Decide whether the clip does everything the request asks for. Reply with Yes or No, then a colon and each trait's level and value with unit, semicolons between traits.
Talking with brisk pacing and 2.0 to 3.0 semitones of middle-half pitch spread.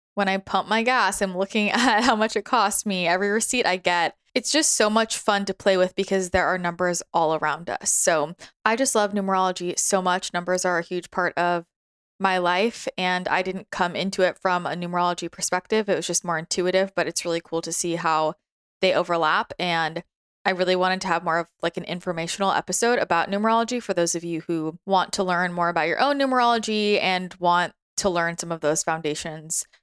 Yes: fast, 215 wpm; average, 2.7 semitones